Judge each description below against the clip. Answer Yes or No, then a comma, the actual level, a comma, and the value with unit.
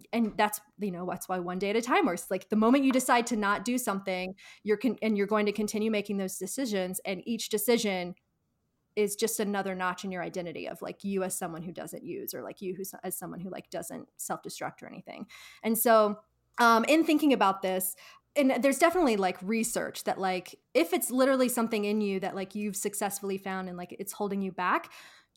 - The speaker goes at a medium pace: No, fast, 220 wpm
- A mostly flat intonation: No, average, 3.4 semitones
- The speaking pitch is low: No, high, 205 Hz